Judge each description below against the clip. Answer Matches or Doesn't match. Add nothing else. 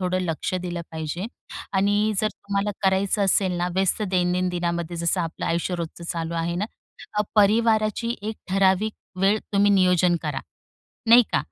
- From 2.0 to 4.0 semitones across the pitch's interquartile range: Matches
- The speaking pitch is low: Doesn't match